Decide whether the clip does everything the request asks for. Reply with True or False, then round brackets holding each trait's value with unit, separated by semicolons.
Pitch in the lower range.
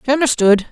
False (250 Hz)